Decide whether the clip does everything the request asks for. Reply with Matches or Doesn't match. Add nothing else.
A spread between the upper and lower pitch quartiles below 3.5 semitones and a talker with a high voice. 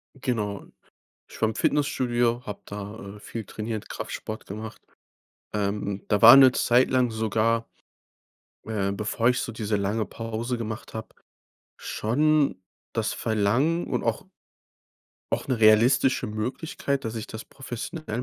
Doesn't match